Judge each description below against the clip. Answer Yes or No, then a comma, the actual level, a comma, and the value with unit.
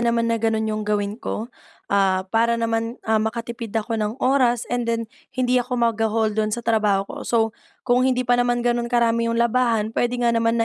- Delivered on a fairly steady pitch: Yes, narrow, 1.5 semitones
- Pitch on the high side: Yes, high, 230 Hz